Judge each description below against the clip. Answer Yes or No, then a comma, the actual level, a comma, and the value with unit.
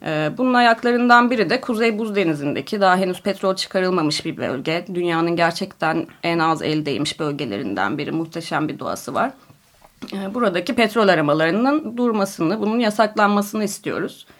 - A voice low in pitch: No, high, 190 Hz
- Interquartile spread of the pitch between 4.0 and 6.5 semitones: Yes, wide, 5.6 semitones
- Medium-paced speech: Yes, average, 130 wpm